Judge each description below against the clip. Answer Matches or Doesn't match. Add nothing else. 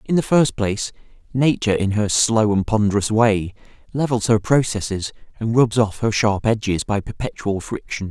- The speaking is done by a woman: Doesn't match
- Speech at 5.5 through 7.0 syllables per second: Doesn't match